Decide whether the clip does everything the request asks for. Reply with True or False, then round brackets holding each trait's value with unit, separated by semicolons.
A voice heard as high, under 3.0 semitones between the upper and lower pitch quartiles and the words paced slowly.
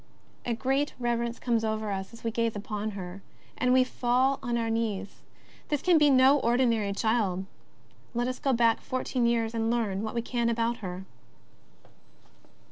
False (235 Hz; 2.4 semitones; 175 wpm)